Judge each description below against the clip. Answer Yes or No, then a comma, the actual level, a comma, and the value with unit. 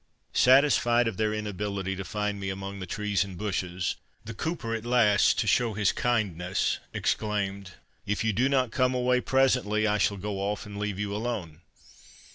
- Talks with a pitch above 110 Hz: No, low, 105 Hz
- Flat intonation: No, average, 3.2 semitones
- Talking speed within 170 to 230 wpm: Yes, average, 175 wpm